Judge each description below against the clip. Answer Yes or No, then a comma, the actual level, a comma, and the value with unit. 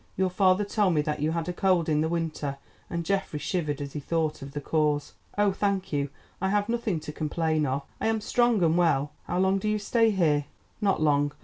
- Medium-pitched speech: Yes, medium, 165 Hz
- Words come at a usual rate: No, fast, 225 wpm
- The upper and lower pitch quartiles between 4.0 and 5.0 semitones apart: Yes, average, 4.6 semitones